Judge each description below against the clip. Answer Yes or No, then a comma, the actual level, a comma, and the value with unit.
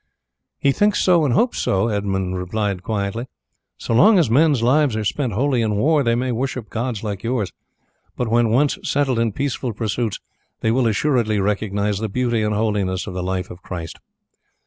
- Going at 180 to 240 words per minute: Yes, average, 185 wpm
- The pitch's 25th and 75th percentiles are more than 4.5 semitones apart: No, average, 4.1 semitones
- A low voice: Yes, low, 115 Hz